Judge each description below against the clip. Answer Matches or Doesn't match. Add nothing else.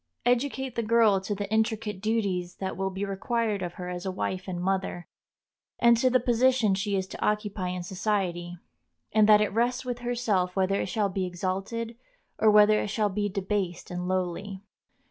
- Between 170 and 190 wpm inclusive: Matches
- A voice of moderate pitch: Doesn't match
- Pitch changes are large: Doesn't match